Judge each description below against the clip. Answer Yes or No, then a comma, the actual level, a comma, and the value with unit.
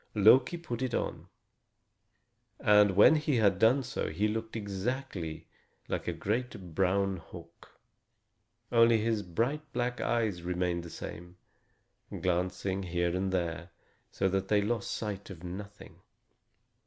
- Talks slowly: Yes, slow, 130 wpm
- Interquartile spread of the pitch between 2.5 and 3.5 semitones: No, average, 4.2 semitones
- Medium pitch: No, low, 100 Hz